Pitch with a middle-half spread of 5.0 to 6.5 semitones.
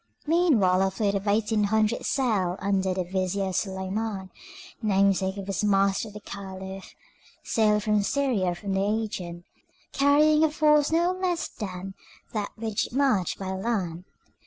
No: average, 3.0 semitones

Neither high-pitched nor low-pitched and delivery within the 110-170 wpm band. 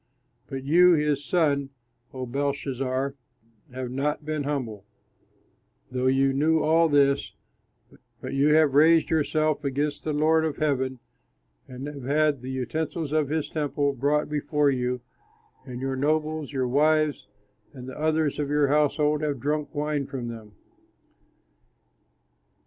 Yes: medium, 145 Hz; average, 140 wpm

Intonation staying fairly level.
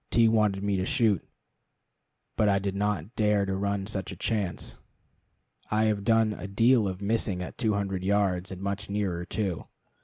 Yes: narrow, 1.9 semitones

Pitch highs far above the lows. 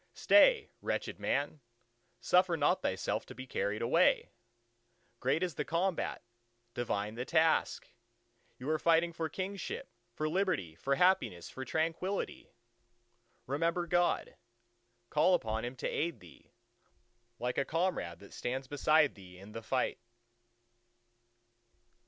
Yes: wide, 6.1 semitones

